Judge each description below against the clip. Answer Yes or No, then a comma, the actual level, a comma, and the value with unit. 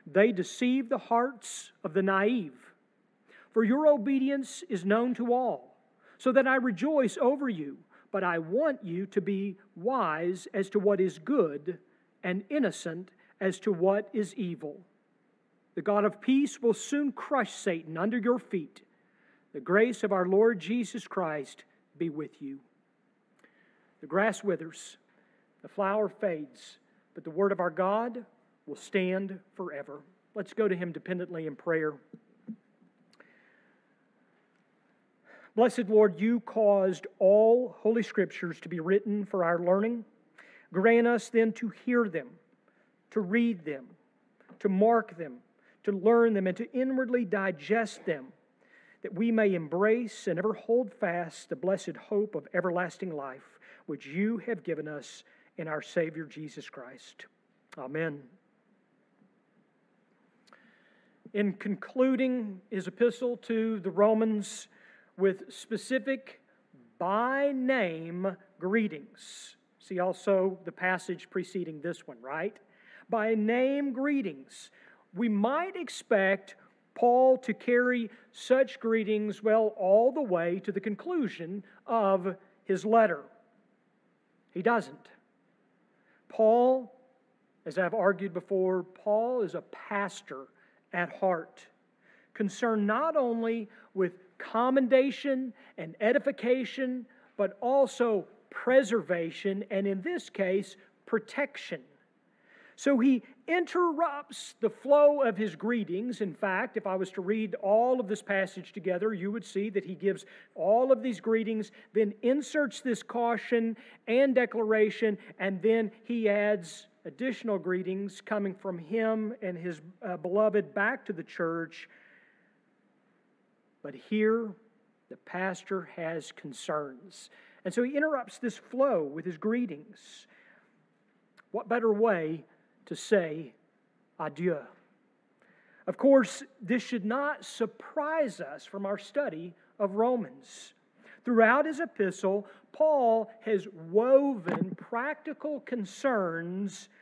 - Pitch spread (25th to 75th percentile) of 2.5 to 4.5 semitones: Yes, average, 4.2 semitones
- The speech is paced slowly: Yes, slow, 125 wpm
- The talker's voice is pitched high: Yes, high, 215 Hz